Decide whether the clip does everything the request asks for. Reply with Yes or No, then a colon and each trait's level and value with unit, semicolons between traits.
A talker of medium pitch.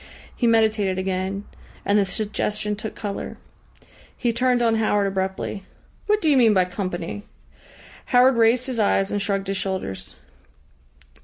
No: high, 205 Hz